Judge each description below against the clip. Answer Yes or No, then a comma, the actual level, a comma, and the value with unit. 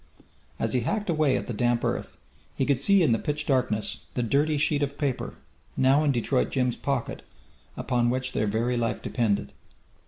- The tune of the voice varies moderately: Yes, average, 3.3 semitones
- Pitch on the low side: Yes, low, 130 Hz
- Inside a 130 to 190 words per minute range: Yes, average, 185 wpm